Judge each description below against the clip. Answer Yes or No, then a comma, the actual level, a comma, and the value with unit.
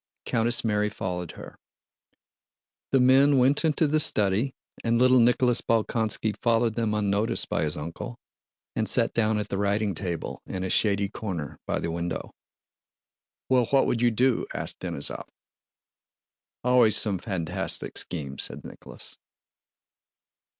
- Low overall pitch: Yes, low, 110 Hz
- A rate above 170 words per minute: No, slow, 135 wpm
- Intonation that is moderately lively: Yes, average, 3.9 semitones